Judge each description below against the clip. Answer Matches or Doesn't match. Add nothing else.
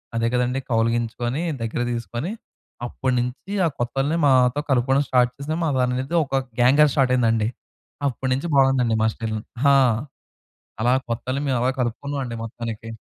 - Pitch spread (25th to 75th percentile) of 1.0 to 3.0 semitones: Matches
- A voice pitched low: Matches